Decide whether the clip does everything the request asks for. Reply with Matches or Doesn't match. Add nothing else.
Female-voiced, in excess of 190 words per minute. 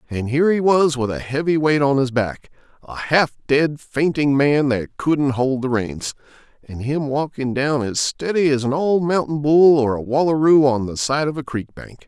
Doesn't match